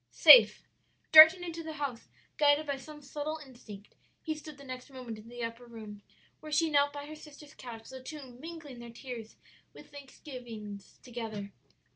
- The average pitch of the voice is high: Yes, very high, 270 Hz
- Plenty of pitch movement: No, average, 4.4 semitones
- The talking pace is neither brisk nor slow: Yes, average, 170 wpm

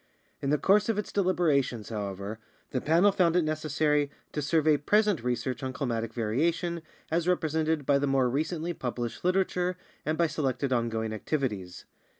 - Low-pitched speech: No, medium, 150 Hz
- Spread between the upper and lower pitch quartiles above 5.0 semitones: Yes, wide, 5.4 semitones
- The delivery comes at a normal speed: Yes, average, 165 wpm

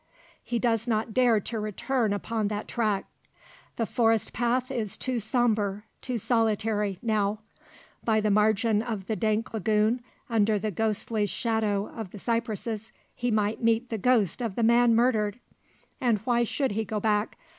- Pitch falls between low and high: No, high, 220 Hz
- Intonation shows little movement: Yes, narrow, 1.9 semitones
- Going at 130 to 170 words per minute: Yes, average, 160 wpm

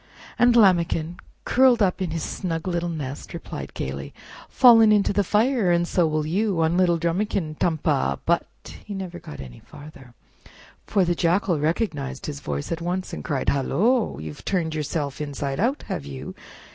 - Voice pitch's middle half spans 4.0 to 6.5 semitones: Yes, average, 4.7 semitones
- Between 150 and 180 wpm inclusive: Yes, average, 170 wpm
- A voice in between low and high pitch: Yes, medium, 170 Hz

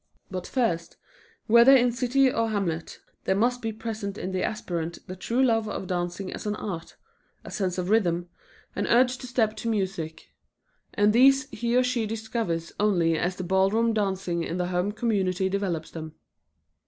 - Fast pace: No, average, 175 wpm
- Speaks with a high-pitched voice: Yes, high, 205 Hz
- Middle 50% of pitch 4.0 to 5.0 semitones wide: Yes, average, 4.4 semitones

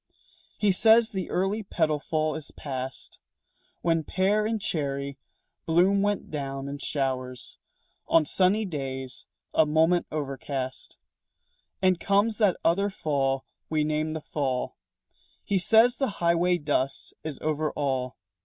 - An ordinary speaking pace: No, slow, 130 wpm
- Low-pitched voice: No, medium, 155 Hz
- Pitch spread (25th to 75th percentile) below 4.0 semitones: No, wide, 5.5 semitones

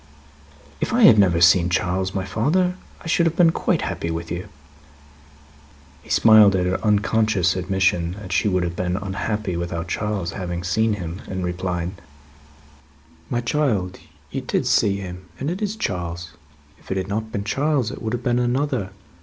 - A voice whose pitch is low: Yes, very low, 95 Hz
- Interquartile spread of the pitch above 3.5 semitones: Yes, average, 4.0 semitones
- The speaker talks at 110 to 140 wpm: No, average, 175 wpm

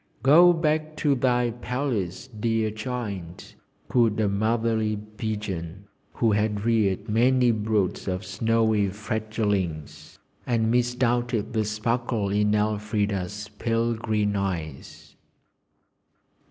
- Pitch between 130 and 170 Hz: No, low, 110 Hz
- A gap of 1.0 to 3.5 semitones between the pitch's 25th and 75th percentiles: Yes, narrow, 2.6 semitones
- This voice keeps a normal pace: No, slow, 100 wpm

